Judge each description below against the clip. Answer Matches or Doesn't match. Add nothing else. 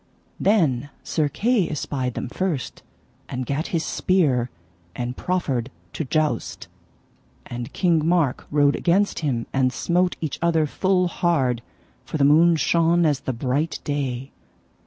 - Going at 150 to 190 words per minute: Doesn't match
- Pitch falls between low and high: Matches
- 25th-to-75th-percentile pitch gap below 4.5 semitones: Doesn't match